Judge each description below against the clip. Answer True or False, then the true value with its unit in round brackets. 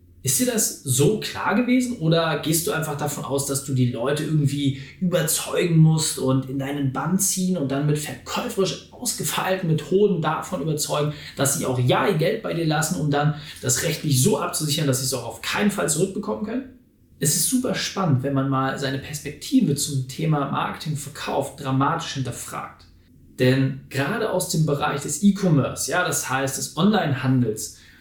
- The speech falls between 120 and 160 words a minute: False (180 wpm)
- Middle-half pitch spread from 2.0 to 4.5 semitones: False (4.9 semitones)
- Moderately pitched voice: True (150 Hz)